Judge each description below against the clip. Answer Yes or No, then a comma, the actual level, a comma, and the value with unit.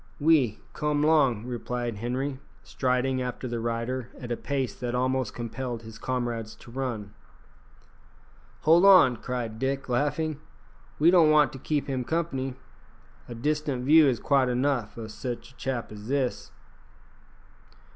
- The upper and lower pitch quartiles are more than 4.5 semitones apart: No, average, 3.1 semitones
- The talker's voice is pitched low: Yes, low, 130 Hz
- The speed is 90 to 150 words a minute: Yes, average, 145 wpm